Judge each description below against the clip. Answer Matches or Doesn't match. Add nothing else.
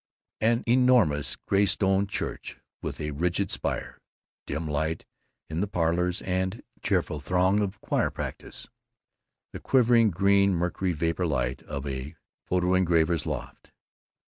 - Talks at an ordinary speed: Doesn't match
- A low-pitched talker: Matches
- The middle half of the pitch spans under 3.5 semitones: Doesn't match